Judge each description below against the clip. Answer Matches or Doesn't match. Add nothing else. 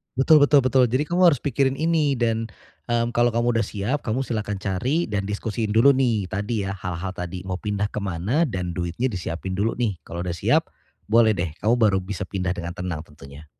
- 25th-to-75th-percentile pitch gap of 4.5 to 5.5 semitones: Matches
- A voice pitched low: Matches